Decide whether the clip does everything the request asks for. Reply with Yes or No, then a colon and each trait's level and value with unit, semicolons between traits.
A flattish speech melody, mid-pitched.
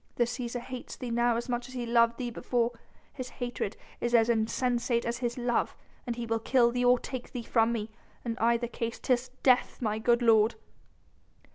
No: narrow, 1.0 semitones; high, 240 Hz